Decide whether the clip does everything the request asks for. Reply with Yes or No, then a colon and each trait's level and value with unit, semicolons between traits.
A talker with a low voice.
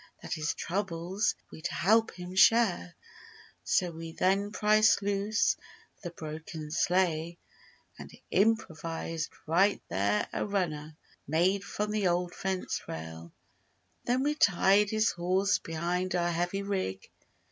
No: medium, 180 Hz